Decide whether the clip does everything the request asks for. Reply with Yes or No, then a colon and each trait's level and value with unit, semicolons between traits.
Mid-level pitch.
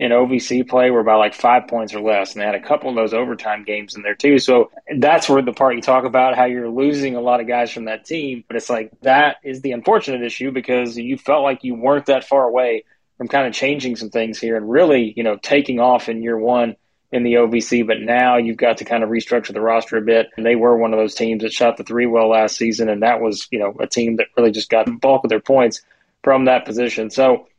No: low, 120 Hz